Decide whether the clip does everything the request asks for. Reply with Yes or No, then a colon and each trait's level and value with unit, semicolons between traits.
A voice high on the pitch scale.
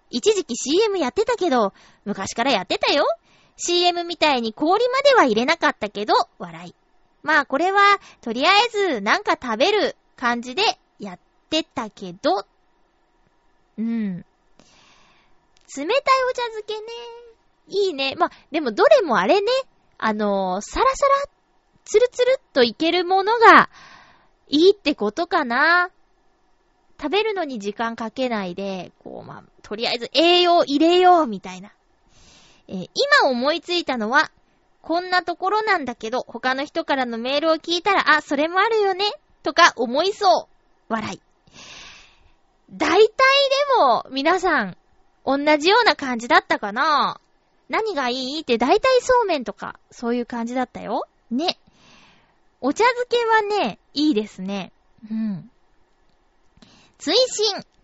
Yes: very high, 310 Hz